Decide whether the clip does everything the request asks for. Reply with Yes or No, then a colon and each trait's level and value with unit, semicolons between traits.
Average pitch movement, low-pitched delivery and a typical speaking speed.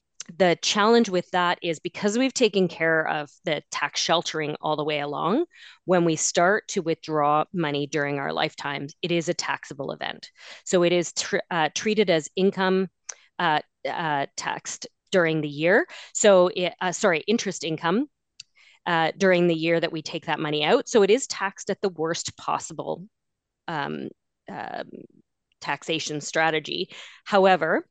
No: average, 3.5 semitones; medium, 175 Hz; average, 160 wpm